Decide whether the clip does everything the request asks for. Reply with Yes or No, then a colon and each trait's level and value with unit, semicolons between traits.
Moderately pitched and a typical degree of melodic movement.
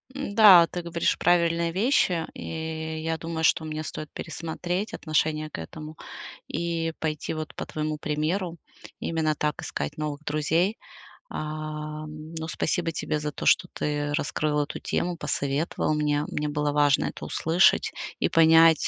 No: medium, 155 Hz; narrow, 1.6 semitones